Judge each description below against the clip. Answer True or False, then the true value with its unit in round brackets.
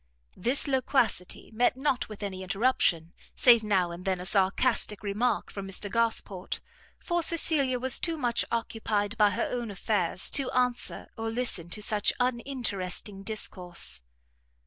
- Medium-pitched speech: False (220 Hz)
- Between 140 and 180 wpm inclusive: True (145 wpm)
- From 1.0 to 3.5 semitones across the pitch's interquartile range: False (4.4 semitones)